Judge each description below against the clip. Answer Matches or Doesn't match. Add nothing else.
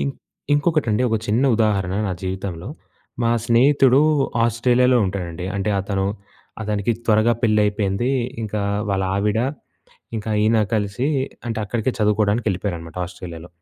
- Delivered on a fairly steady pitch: Doesn't match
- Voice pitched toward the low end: Matches